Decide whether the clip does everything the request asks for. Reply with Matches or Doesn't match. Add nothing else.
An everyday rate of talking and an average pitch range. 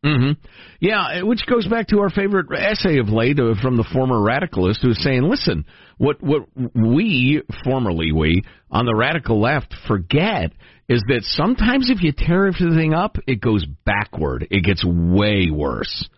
Doesn't match